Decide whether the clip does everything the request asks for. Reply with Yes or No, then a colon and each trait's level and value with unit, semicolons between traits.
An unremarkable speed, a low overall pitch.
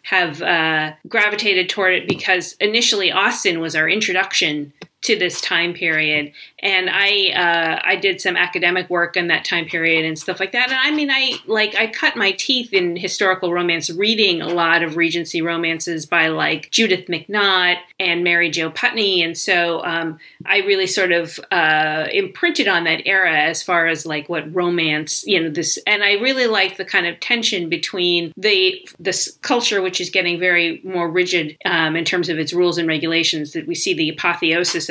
No: average, 185 wpm; medium, 175 Hz